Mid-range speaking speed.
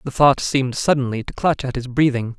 No: fast, 225 wpm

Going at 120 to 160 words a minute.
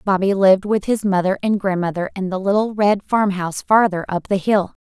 No: average, 200 wpm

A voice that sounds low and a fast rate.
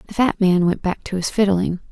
No: high, 190 Hz; fast, 250 wpm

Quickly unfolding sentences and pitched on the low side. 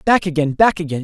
No: fast, 230 wpm; medium, 170 Hz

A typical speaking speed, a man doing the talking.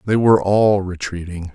Yes: average, 155 wpm; male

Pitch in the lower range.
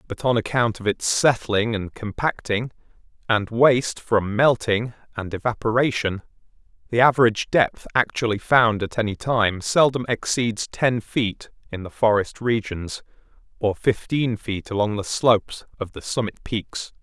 Yes: low, 115 Hz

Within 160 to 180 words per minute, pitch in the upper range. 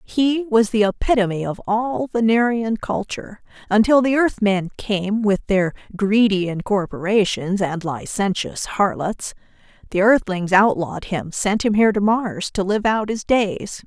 No: average, 145 wpm; high, 210 Hz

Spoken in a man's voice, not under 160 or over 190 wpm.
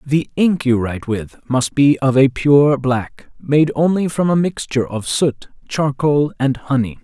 Yes: male; average, 180 wpm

